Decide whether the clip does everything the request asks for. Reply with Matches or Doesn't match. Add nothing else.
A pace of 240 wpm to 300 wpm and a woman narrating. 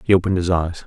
Doesn't match